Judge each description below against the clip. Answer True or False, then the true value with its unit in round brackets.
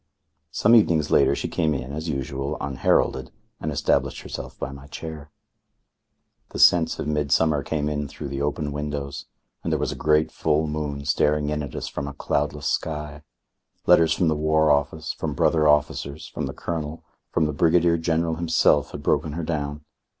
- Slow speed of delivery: False (180 wpm)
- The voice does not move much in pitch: True (1.6 semitones)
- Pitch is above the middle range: False (75 Hz)